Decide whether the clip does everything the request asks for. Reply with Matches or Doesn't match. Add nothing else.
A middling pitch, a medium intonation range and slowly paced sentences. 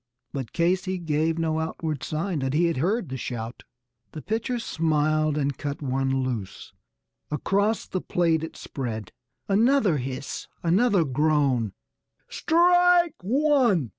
Doesn't match